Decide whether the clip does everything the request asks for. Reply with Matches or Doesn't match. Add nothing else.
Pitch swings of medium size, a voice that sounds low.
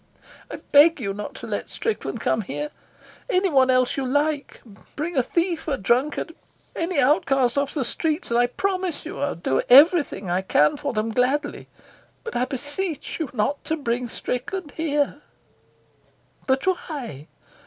Doesn't match